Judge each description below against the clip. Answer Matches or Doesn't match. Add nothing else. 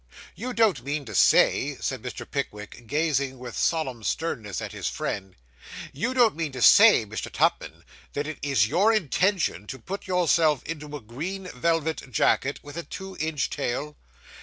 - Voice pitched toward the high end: Doesn't match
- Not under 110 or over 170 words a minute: Matches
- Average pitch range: Doesn't match